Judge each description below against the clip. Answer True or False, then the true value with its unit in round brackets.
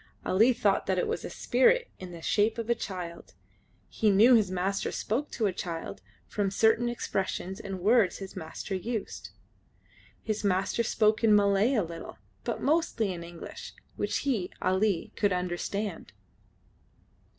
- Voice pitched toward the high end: True (200 Hz)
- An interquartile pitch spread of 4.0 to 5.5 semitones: False (3.3 semitones)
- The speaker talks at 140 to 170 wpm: True (155 wpm)